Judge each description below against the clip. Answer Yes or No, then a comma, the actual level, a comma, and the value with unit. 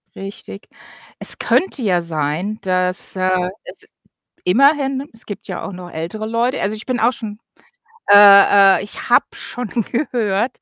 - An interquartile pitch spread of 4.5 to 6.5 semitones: Yes, average, 4.8 semitones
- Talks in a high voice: Yes, high, 210 Hz